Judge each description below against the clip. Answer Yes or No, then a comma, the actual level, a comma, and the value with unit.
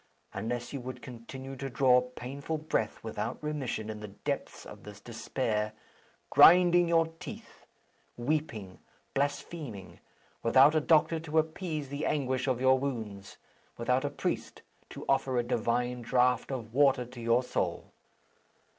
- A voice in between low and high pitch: No, low, 125 Hz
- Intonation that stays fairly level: No, average, 3.7 semitones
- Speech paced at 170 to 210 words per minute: No, average, 140 wpm